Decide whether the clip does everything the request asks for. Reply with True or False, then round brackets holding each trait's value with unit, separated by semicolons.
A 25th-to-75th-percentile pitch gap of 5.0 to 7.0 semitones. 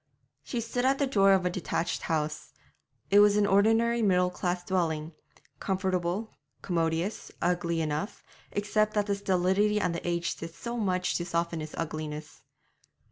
False (3.4 semitones)